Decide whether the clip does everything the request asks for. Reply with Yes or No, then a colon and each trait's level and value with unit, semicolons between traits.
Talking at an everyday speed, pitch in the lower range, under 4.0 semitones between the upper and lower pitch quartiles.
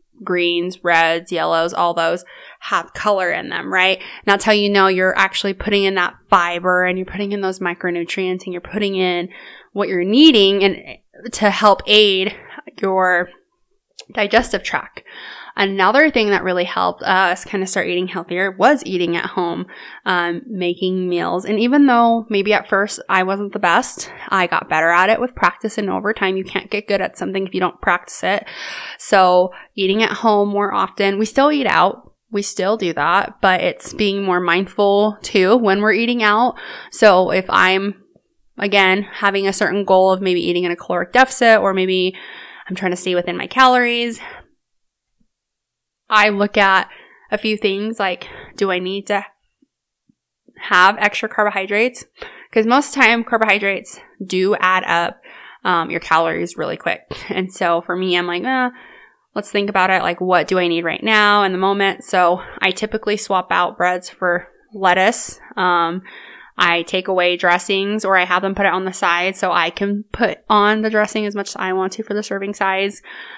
No: average, 185 wpm; high, 195 Hz; narrow, 2.5 semitones